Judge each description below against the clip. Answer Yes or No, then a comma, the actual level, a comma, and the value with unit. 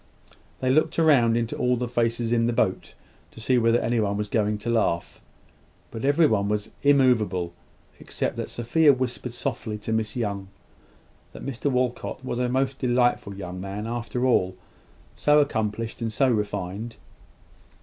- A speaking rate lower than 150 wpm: No, average, 155 wpm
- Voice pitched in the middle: No, low, 115 Hz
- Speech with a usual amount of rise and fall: Yes, average, 3.1 semitones